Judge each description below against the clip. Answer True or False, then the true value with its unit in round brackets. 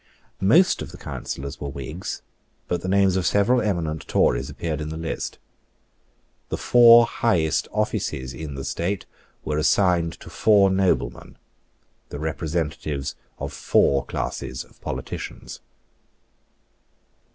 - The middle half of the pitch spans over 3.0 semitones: True (5.2 semitones)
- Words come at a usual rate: False (125 wpm)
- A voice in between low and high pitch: False (80 Hz)